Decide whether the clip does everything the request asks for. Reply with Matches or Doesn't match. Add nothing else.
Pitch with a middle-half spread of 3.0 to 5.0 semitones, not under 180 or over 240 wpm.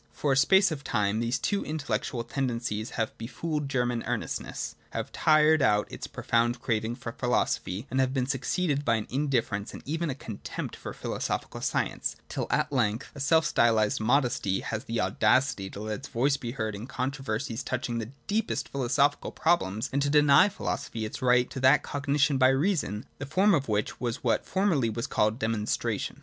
Matches